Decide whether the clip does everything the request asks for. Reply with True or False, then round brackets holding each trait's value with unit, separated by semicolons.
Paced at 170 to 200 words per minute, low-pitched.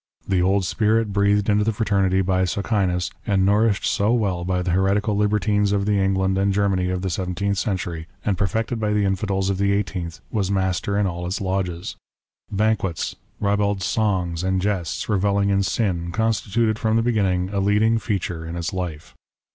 True (180 wpm; 100 Hz)